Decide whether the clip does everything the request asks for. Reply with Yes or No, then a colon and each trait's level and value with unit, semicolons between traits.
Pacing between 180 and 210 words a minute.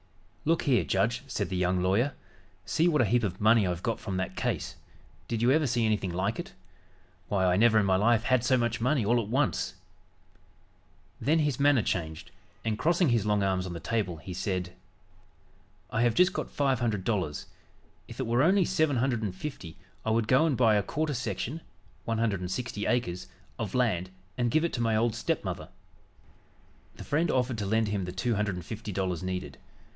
Yes: average, 200 wpm